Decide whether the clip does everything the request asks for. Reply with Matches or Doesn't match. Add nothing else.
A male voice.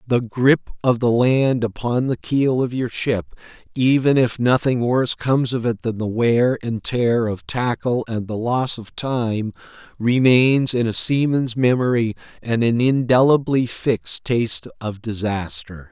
Matches